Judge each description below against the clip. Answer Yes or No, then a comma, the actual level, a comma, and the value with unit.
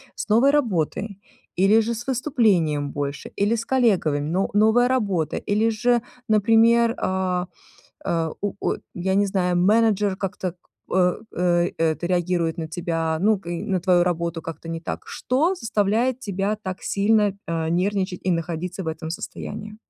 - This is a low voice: No, high, 190 Hz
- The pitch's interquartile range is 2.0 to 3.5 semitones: No, average, 4.3 semitones